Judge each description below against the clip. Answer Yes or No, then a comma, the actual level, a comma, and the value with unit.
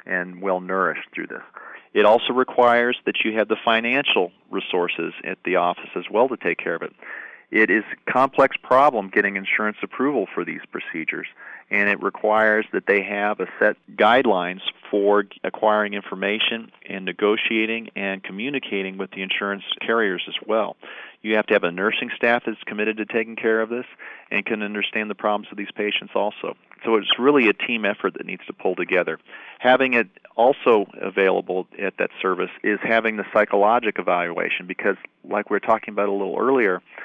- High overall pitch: No, low, 105 Hz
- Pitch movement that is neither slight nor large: No, narrow, 2.2 semitones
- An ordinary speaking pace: Yes, average, 180 wpm